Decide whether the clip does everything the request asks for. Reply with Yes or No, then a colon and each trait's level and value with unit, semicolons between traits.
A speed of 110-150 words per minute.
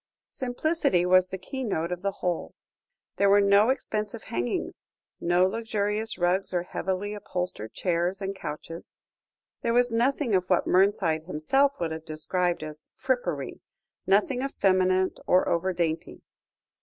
Yes: slow, 135 wpm